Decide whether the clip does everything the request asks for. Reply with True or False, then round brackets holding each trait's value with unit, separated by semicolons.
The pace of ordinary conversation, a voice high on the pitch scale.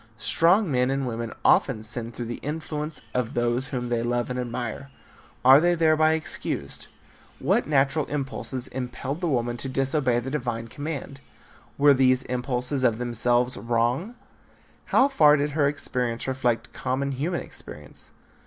False (150 wpm; 130 Hz)